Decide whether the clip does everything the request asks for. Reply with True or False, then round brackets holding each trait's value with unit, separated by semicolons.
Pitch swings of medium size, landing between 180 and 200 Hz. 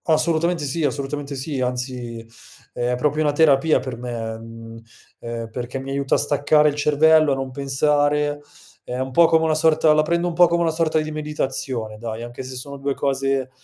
False (3.5 semitones; 140 Hz)